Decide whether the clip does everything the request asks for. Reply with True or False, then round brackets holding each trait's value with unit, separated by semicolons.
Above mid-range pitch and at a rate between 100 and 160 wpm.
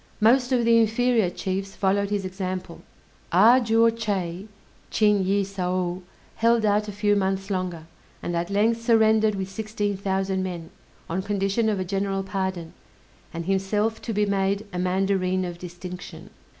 True (195 Hz; 155 wpm)